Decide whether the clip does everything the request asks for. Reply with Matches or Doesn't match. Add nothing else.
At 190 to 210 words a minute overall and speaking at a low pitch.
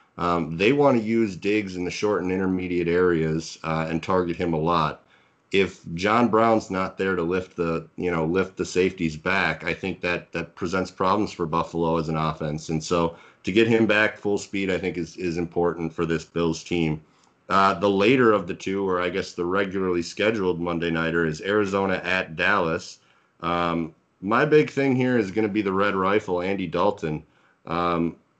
Matches